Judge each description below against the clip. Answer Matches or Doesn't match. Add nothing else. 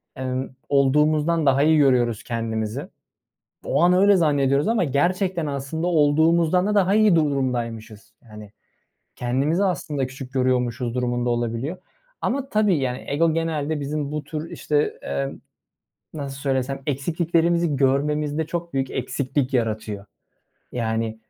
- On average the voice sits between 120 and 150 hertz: Matches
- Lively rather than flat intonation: Doesn't match